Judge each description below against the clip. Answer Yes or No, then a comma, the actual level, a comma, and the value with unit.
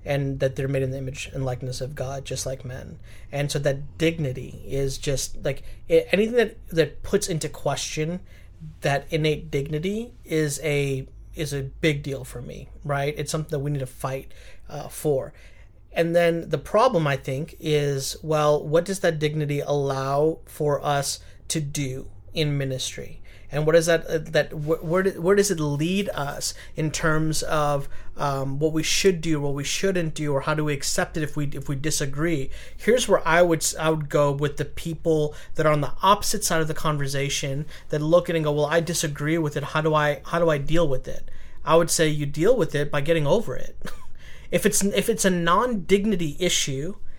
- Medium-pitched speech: Yes, medium, 150 Hz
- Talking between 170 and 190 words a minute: No, average, 200 wpm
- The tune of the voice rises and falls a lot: No, average, 3.1 semitones